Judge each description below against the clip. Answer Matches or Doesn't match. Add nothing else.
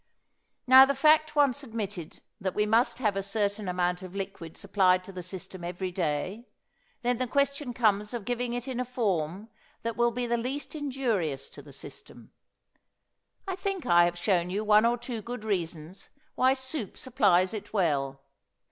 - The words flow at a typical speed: Matches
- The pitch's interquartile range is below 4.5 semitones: Doesn't match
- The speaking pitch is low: Doesn't match